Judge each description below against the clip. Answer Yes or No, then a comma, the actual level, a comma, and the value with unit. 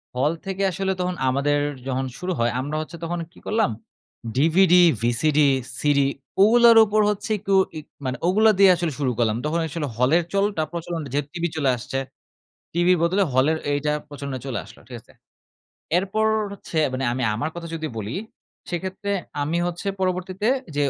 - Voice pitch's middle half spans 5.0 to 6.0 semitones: Yes, average, 5.3 semitones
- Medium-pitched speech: Yes, medium, 165 Hz